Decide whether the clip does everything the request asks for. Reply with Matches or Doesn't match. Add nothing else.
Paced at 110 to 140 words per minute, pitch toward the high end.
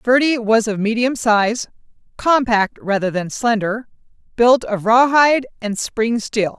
Matches